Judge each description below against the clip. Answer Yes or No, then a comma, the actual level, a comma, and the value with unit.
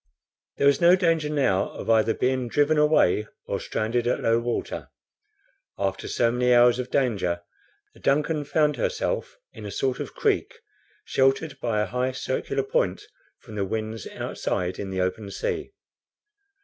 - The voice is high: No, low, 125 Hz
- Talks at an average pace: Yes, average, 160 wpm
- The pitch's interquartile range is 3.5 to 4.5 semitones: No, average, 5.1 semitones